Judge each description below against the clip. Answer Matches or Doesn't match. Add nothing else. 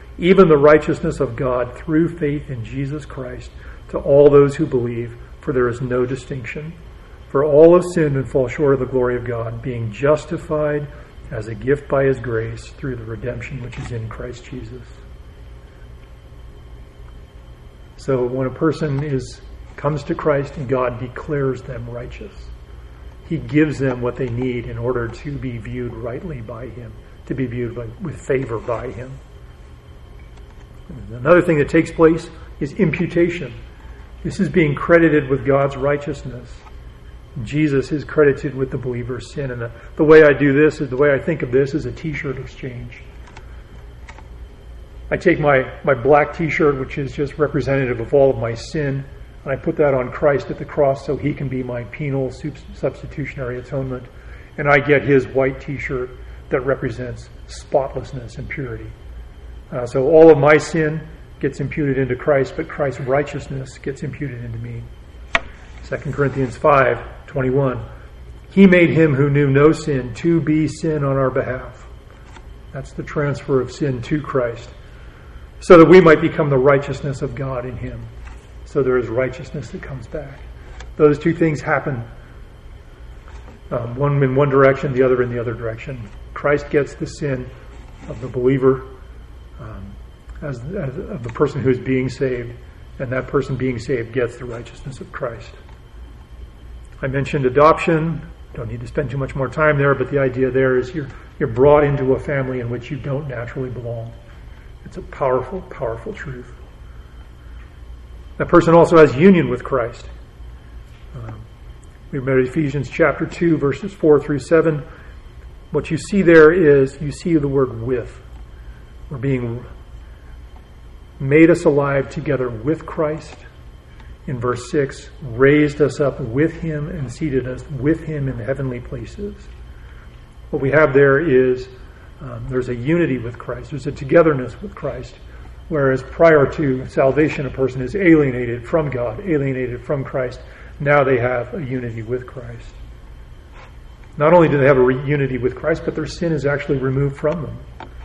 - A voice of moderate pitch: Doesn't match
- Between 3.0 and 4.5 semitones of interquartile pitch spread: Matches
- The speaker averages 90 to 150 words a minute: Doesn't match